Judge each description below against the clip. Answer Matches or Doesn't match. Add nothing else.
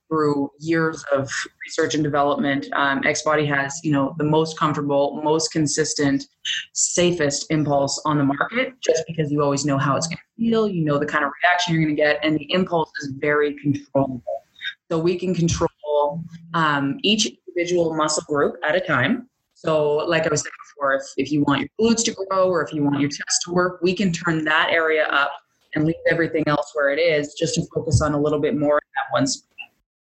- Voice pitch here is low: Doesn't match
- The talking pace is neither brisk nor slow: Doesn't match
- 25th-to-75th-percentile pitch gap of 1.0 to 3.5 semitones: Matches